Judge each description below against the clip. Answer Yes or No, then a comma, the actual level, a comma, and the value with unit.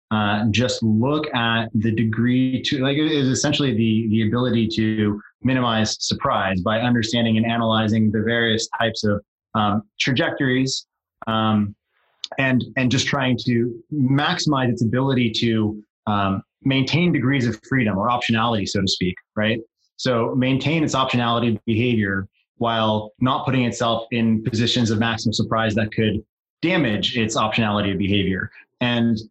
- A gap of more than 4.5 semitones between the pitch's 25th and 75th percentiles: No, narrow, 2.6 semitones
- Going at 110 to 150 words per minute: Yes, average, 145 wpm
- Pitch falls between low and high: No, low, 115 Hz